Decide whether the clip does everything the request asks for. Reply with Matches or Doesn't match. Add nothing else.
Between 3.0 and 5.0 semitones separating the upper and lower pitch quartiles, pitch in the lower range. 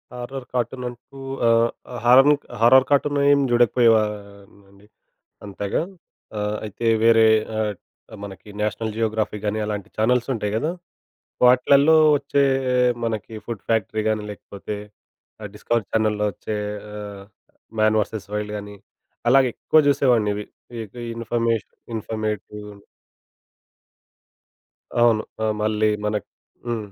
Doesn't match